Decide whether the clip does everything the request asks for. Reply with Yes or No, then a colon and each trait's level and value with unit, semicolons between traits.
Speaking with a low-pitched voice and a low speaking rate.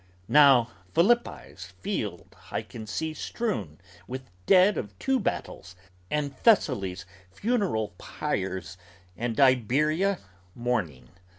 Yes: low, 125 Hz; slow, 100 wpm